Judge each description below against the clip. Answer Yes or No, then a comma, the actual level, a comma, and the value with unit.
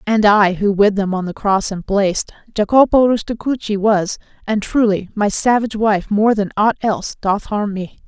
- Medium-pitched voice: No, high, 210 Hz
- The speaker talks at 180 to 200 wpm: Yes, average, 185 wpm